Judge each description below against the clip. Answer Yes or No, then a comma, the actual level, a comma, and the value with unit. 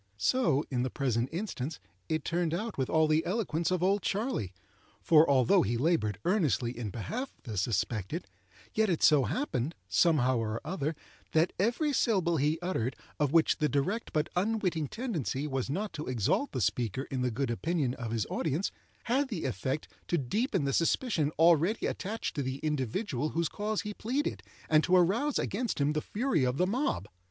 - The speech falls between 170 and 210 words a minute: Yes, average, 180 wpm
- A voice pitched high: No, medium, 155 Hz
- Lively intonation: Yes, wide, 7.2 semitones